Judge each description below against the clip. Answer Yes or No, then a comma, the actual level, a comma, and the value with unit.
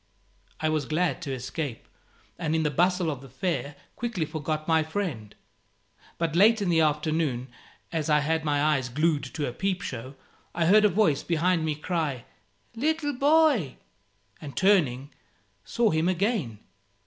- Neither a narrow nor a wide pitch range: Yes, average, 4.0 semitones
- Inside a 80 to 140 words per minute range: No, average, 160 wpm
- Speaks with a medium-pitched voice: Yes, medium, 160 Hz